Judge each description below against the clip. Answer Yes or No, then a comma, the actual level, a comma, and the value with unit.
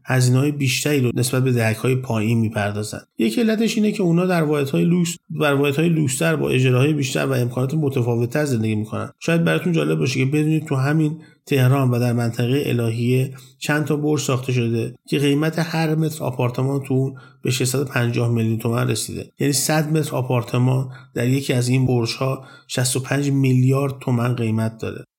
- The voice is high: No, low, 135 Hz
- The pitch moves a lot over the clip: No, average, 3.5 semitones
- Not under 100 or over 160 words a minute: No, fast, 170 wpm